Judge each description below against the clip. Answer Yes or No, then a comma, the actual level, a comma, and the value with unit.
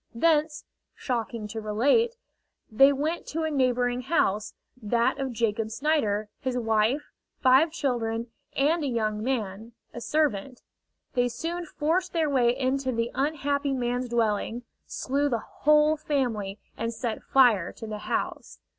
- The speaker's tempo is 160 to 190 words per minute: No, average, 140 wpm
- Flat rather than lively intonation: No, average, 4.5 semitones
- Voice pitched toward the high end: Yes, very high, 250 Hz